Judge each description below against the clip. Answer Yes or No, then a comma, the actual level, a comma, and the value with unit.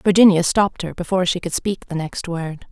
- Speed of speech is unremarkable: No, fast, 220 wpm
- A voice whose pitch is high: No, medium, 180 Hz